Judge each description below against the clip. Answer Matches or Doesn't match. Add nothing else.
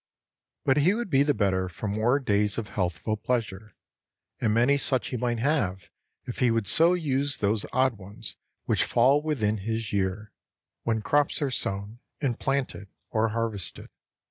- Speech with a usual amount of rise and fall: Matches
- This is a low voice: Matches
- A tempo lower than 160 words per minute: Doesn't match